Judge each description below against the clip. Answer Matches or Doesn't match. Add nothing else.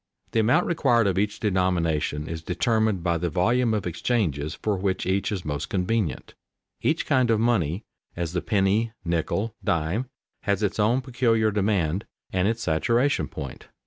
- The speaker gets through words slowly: Doesn't match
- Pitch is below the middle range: Matches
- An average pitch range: Matches